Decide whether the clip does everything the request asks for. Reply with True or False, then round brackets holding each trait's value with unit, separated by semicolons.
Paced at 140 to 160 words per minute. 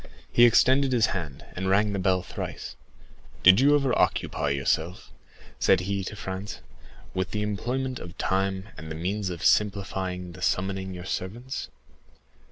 True (155 wpm)